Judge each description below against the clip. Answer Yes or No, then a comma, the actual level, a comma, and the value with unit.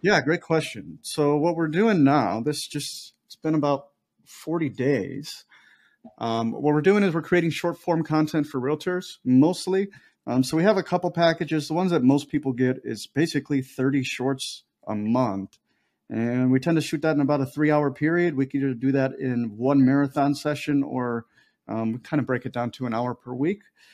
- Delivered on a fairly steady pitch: No, average, 3.9 semitones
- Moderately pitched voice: Yes, medium, 145 Hz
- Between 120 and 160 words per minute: No, average, 200 wpm